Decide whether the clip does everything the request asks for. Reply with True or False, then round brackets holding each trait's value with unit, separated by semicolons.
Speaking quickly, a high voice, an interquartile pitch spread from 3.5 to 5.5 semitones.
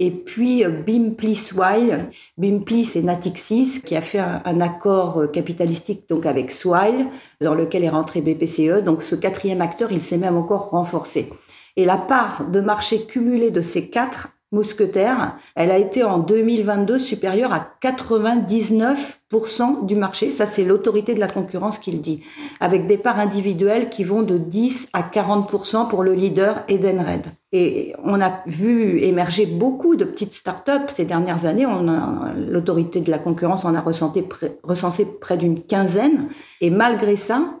False (160 wpm; 200 Hz; 4.5 semitones)